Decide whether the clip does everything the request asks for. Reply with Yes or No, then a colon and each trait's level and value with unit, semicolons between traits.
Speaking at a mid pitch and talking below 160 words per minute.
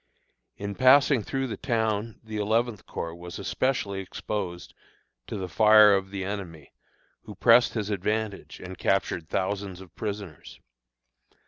No: low, 100 Hz; slow, 135 wpm